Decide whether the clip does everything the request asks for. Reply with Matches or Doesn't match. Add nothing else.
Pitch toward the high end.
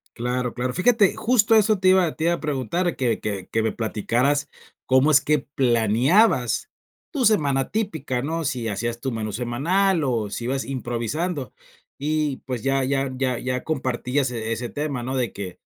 Doesn't match